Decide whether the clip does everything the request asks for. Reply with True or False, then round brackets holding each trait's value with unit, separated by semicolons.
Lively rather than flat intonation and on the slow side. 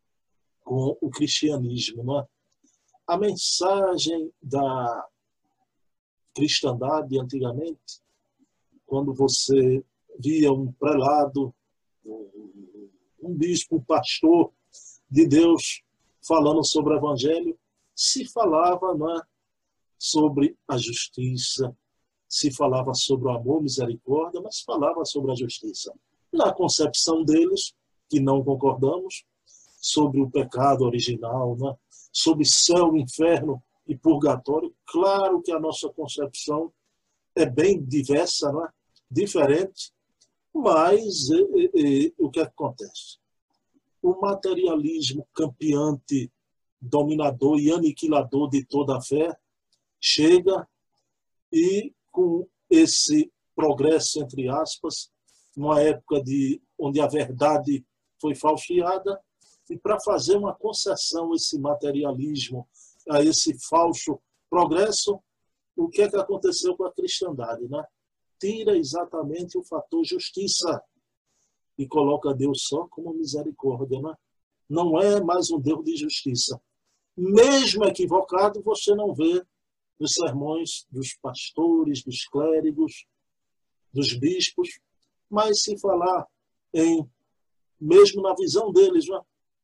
True (6.1 semitones; 110 wpm)